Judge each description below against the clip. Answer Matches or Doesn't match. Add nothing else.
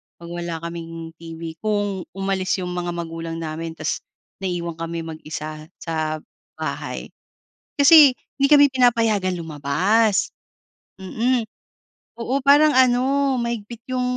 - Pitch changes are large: Matches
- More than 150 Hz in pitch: Matches